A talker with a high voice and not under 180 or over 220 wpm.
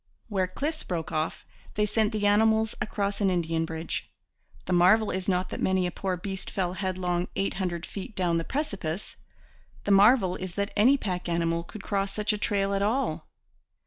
Yes: high, 195 Hz; average, 185 wpm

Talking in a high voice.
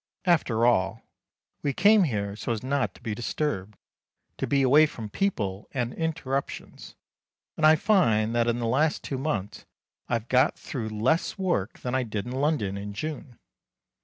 No: low, 125 Hz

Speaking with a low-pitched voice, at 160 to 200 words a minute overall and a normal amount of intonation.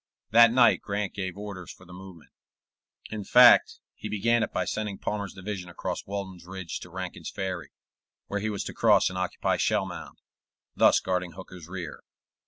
No: very low, 95 Hz; average, 170 wpm; narrow, 2.3 semitones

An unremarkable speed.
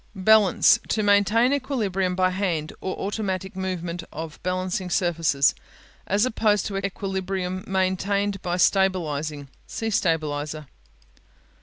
No: slow, 110 wpm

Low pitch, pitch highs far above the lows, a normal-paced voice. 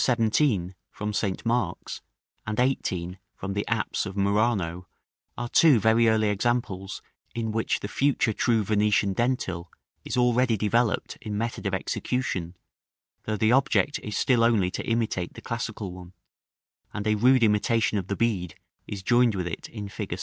No: low, 110 Hz; average, 3.3 semitones; average, 160 wpm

